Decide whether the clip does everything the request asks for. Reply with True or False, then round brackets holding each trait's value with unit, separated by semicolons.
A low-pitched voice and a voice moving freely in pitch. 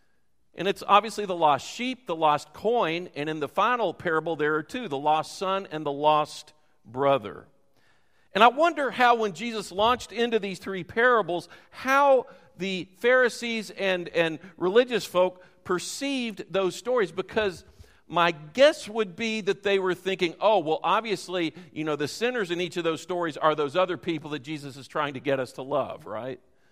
False (180 Hz; 5.9 semitones)